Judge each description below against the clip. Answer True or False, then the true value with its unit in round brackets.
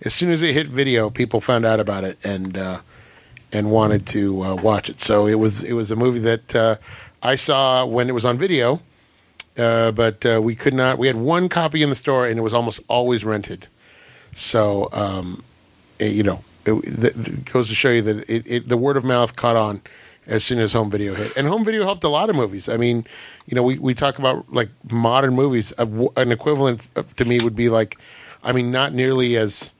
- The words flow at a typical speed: False (230 wpm)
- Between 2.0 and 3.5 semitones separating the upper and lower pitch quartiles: True (2.9 semitones)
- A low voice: True (120 Hz)